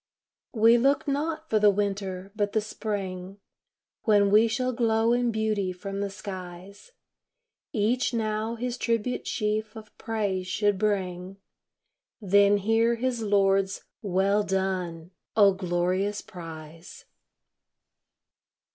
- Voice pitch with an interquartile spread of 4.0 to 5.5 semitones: No, average, 2.8 semitones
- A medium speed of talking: No, slow, 115 wpm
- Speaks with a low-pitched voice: No, high, 205 Hz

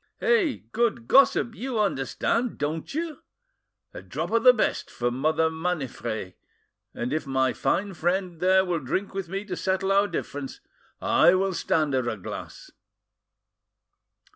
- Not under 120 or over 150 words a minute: Yes, average, 145 wpm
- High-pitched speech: No, medium, 180 Hz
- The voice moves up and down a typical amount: No, wide, 6.7 semitones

